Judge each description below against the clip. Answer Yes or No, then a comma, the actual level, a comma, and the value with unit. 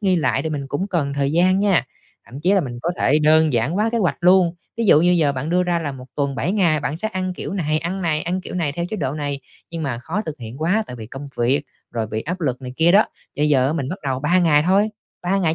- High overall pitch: No, medium, 160 Hz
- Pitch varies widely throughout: No, average, 4.5 semitones